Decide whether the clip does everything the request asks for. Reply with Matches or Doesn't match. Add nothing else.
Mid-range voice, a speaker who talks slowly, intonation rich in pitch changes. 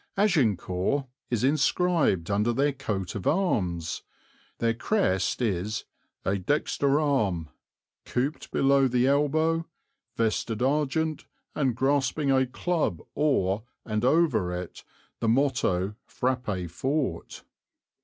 Doesn't match